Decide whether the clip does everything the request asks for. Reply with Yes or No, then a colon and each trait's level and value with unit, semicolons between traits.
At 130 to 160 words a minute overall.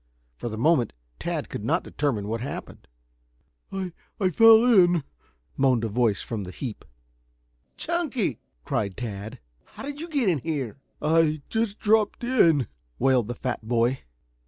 Yes: average, 155 wpm